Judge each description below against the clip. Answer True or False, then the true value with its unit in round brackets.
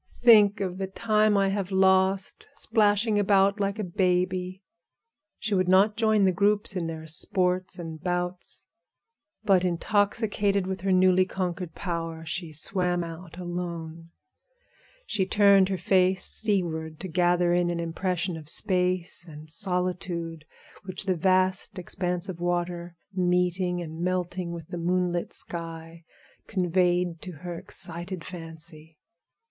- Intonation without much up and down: True (2.0 semitones)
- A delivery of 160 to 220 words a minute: False (135 wpm)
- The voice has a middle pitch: True (180 Hz)